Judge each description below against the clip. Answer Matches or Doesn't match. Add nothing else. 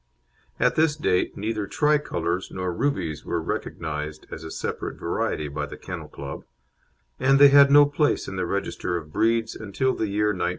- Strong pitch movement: Matches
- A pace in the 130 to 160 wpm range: Doesn't match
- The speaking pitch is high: Doesn't match